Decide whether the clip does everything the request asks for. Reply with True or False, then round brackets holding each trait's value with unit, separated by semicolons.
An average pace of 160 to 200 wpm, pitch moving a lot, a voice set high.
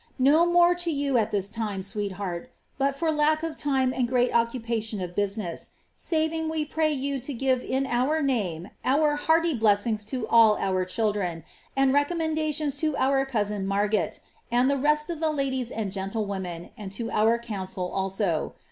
True (175 wpm; 6.2 semitones; 245 Hz)